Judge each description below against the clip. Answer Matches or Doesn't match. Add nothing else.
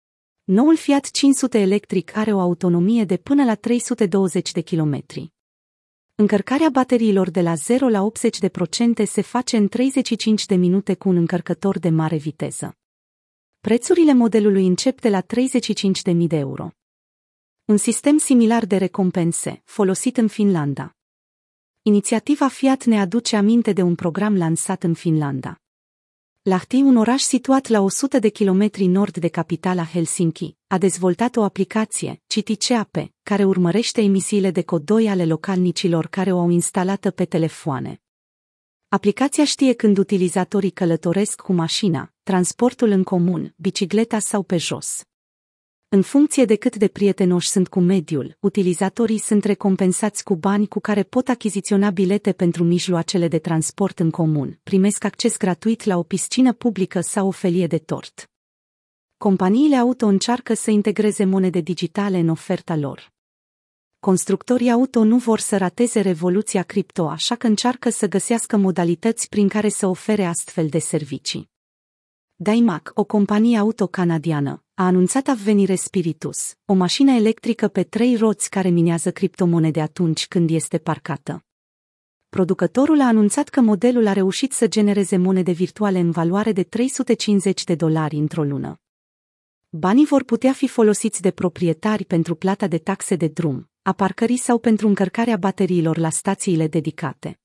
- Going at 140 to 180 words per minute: Matches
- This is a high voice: Matches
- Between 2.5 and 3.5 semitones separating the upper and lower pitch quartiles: Doesn't match